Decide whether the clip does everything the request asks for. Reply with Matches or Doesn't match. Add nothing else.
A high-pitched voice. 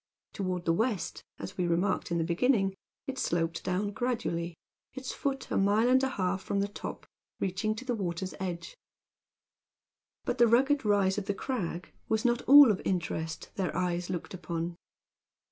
Matches